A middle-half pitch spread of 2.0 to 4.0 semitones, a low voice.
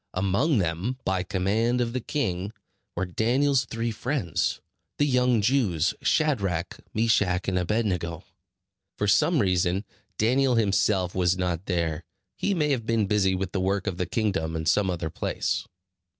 No: average, 4.7 semitones; low, 100 Hz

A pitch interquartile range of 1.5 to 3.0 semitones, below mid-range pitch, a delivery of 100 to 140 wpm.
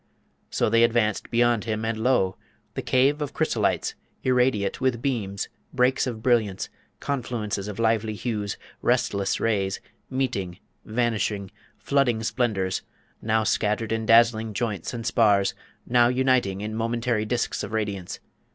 Yes: narrow, 2.6 semitones; low, 115 Hz; slow, 135 wpm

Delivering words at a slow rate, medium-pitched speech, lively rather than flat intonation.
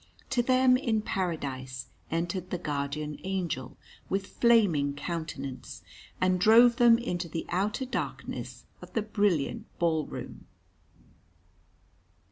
Yes: slow, 110 wpm; medium, 180 Hz; wide, 6.4 semitones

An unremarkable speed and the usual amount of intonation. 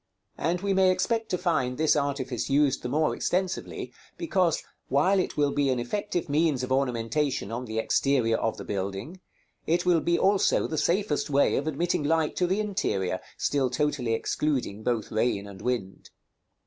No: average, 175 wpm; wide, 6.1 semitones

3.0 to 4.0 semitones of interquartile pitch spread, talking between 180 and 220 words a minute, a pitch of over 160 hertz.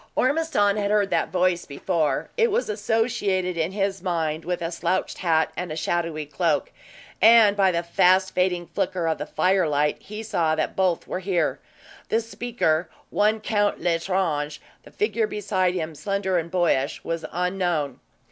No: average, 3.5 semitones; average, 155 wpm; medium, 185 Hz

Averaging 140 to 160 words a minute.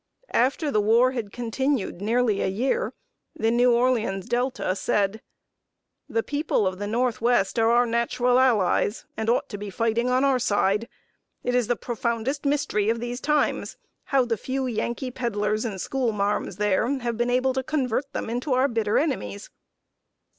No: average, 170 wpm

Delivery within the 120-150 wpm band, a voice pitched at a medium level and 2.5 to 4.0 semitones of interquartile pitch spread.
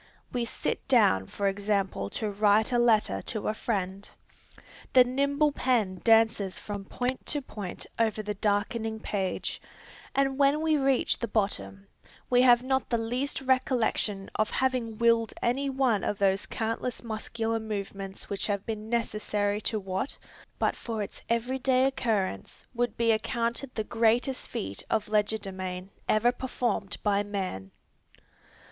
No: average, 145 wpm; high, 220 Hz; average, 3.5 semitones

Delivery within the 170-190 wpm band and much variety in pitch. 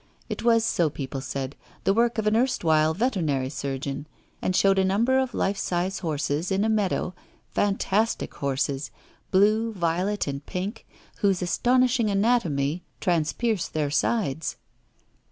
No: slow, 135 wpm; wide, 6.4 semitones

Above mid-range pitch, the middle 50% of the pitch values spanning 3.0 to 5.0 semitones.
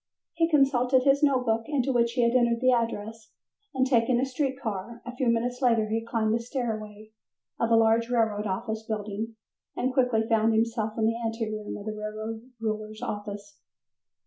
No: high, 230 Hz; narrow, 2.4 semitones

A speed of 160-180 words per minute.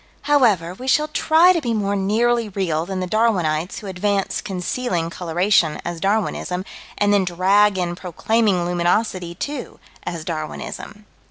No: average, 145 wpm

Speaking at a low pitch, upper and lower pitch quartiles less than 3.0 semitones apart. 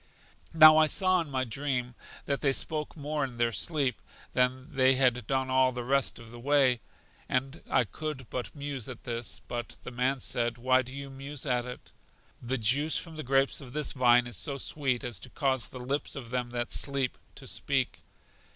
Yes: low, 130 Hz; narrow, 2.5 semitones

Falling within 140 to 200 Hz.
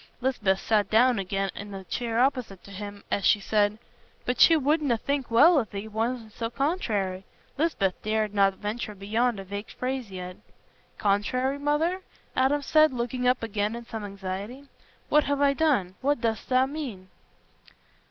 No: high, 230 Hz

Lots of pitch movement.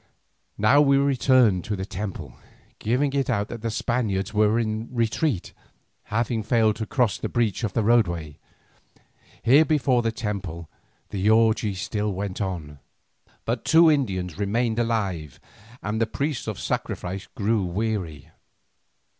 No: average, 3.6 semitones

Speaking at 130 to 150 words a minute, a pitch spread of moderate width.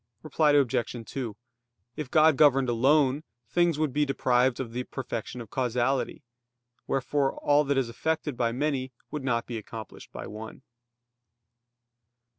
Yes: average, 140 wpm; average, 3.5 semitones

